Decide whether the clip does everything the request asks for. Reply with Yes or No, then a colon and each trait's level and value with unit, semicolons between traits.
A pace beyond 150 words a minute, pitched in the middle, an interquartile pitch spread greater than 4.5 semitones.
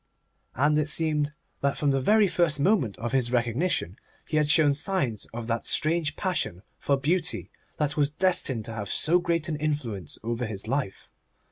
Yes: average, 175 wpm; medium, 145 Hz; average, 5.2 semitones